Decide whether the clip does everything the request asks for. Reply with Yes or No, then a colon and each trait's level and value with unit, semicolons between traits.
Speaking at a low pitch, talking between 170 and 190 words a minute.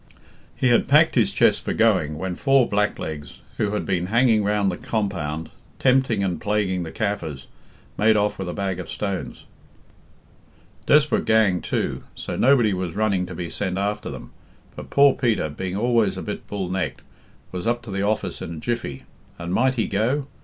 Yes: low, 100 Hz; average, 180 wpm